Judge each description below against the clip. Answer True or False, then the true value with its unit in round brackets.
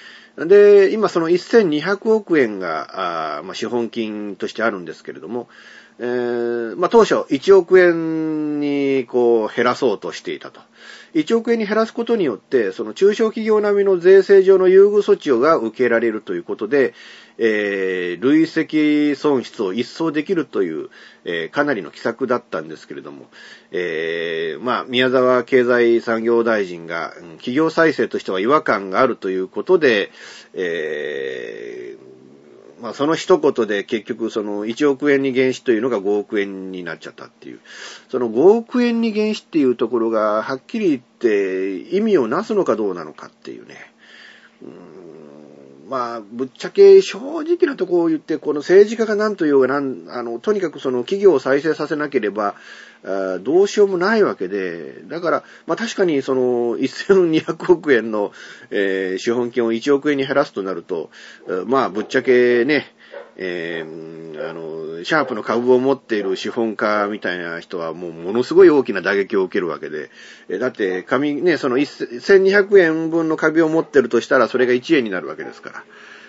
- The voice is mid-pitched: True (155 Hz)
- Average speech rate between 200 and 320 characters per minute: True (315 characters per minute)